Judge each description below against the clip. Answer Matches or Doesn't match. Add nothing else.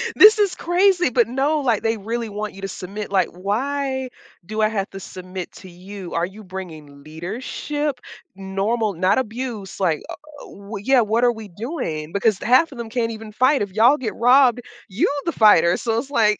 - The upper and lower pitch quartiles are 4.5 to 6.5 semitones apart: Matches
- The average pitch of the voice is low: Doesn't match